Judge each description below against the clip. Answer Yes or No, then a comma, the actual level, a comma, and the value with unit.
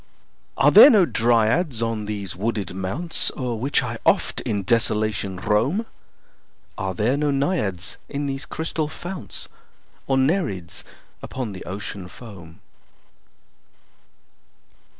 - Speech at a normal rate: No, slow, 115 wpm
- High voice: No, low, 115 Hz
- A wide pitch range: Yes, wide, 6.5 semitones